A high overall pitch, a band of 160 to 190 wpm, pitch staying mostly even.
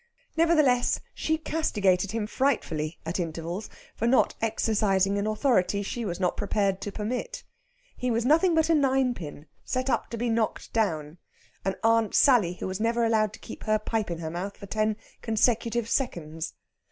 No: high, 215 Hz; average, 170 wpm; average, 4.5 semitones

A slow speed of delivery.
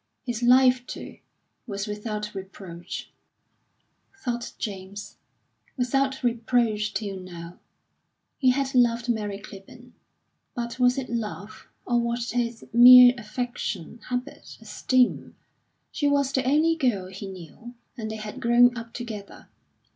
Yes: slow, 125 wpm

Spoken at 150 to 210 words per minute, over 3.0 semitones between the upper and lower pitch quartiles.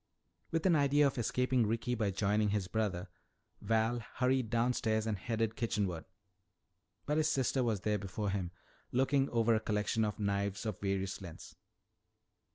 Yes: average, 155 wpm; average, 3.6 semitones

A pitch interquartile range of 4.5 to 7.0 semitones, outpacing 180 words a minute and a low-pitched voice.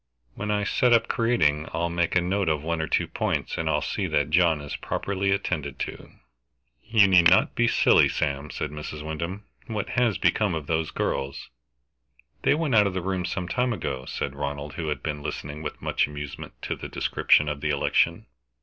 Yes: average, 5.1 semitones; average, 200 wpm; very low, 80 Hz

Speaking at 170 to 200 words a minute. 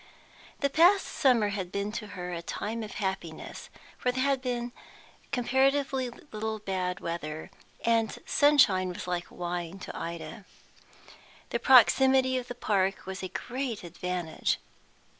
No: average, 140 wpm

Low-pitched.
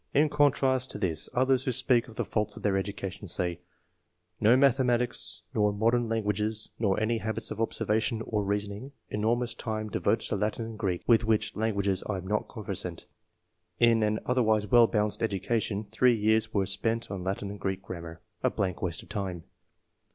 Yes: low, 110 Hz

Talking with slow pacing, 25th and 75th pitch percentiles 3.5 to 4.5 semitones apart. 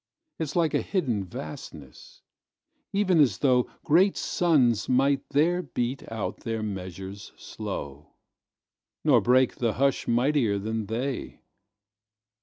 No: slow, 105 wpm; wide, 5.4 semitones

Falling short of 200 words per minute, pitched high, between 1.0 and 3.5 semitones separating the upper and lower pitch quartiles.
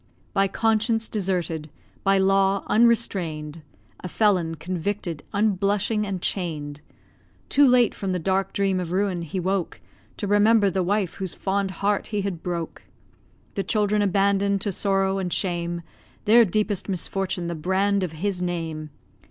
Yes: average, 145 wpm; high, 195 Hz; narrow, 2.6 semitones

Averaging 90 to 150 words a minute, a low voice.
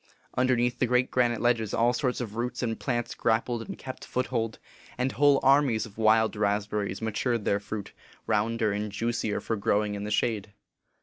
No: average, 180 wpm; low, 115 Hz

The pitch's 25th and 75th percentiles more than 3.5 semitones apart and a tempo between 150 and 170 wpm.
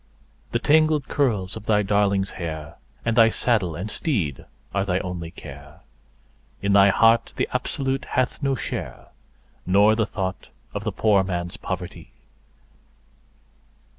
No: average, 4.0 semitones; slow, 135 wpm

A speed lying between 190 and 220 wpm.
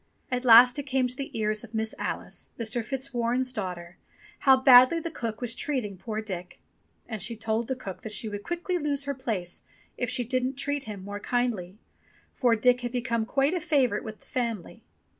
Yes: average, 195 wpm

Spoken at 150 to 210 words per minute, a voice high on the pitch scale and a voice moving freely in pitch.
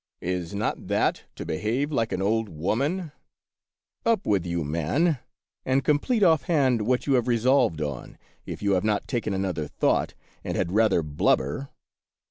No: average, 160 wpm; low, 110 Hz; wide, 7.6 semitones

